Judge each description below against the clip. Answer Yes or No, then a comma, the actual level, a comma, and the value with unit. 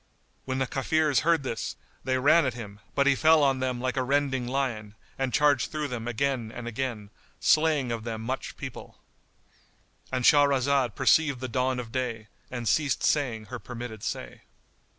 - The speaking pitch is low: Yes, low, 130 Hz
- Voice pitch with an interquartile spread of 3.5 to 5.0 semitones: No, average, 2.9 semitones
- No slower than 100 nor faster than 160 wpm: No, average, 170 wpm